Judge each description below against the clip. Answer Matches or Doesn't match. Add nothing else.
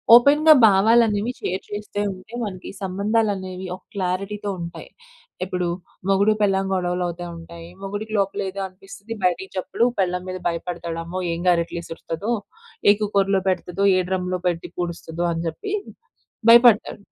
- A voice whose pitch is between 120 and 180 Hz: Doesn't match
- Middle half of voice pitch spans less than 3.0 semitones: Matches